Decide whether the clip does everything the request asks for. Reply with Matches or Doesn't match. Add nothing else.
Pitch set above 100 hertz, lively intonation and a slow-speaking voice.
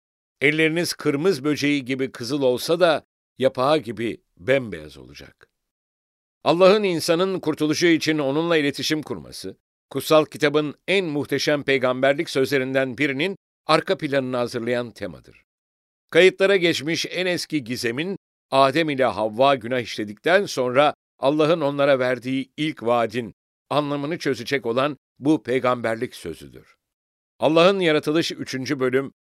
Doesn't match